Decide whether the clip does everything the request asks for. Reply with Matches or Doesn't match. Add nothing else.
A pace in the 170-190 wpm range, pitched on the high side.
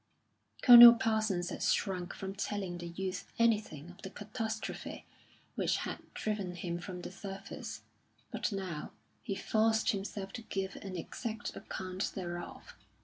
Doesn't match